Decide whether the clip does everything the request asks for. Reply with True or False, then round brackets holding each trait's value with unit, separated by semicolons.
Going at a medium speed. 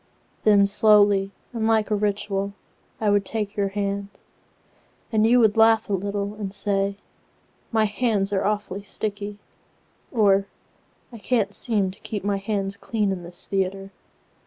False (130 wpm)